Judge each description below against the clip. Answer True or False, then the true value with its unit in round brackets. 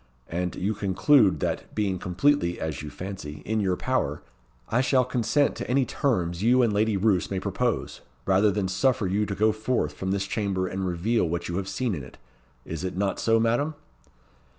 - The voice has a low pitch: True (100 Hz)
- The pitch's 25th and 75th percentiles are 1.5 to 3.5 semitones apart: False (3.9 semitones)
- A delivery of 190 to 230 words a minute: True (195 wpm)